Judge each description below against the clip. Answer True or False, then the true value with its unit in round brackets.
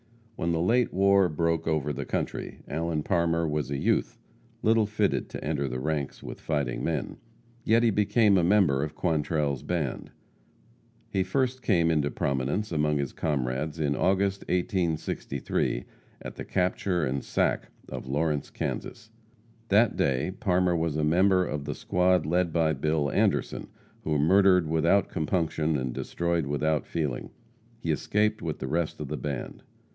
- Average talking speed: True (155 wpm)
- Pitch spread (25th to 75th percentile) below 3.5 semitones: False (3.9 semitones)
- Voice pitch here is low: True (80 Hz)